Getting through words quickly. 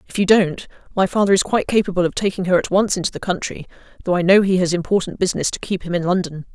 Yes: fast, 255 wpm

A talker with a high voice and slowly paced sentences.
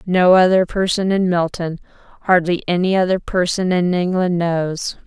No: medium, 180 Hz; slow, 130 wpm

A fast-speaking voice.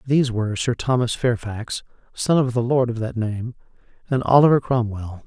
No: average, 170 wpm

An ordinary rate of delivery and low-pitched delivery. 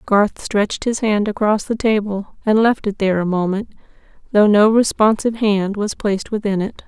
No: average, 185 wpm; high, 210 Hz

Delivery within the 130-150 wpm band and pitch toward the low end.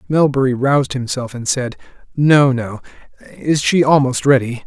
Yes: average, 140 wpm; low, 130 Hz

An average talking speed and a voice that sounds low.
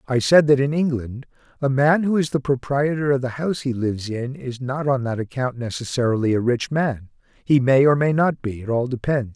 No: fast, 225 wpm; low, 130 Hz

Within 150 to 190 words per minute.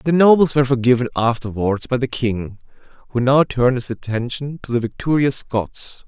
Yes: average, 170 wpm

